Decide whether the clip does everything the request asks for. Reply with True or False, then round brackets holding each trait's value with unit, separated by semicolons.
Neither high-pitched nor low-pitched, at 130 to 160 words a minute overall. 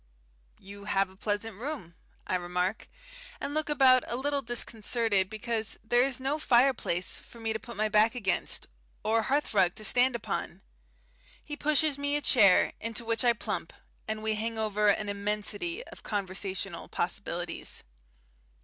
False (220 Hz; 155 wpm)